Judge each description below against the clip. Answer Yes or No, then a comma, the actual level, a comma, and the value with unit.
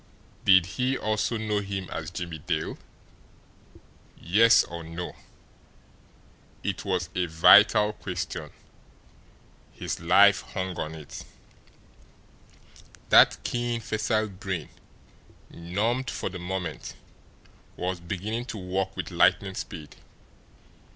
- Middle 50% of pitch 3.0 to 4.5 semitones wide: Yes, average, 3.6 semitones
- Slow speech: Yes, slow, 105 wpm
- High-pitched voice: No, very low, 95 Hz